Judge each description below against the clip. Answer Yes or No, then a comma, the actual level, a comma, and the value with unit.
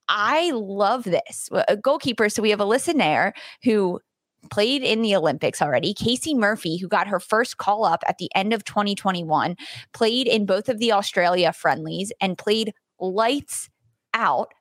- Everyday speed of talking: Yes, average, 165 wpm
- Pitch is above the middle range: Yes, high, 210 Hz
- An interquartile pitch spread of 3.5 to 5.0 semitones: Yes, average, 3.8 semitones